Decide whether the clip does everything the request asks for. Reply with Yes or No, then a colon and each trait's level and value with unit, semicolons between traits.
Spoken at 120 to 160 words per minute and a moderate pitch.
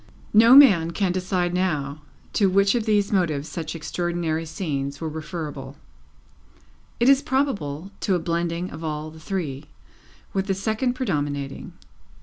Yes: average, 140 wpm; medium, 175 Hz